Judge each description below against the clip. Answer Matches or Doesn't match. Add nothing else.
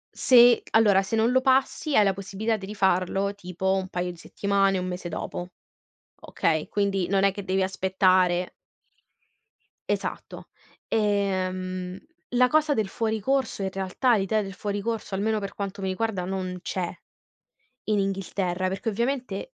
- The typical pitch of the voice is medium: Doesn't match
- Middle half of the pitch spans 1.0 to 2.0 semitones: Doesn't match